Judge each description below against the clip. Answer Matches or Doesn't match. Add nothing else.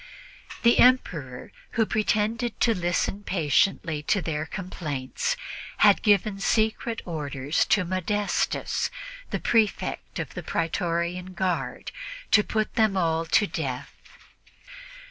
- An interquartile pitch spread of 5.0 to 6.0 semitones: Doesn't match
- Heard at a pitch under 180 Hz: Doesn't match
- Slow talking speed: Matches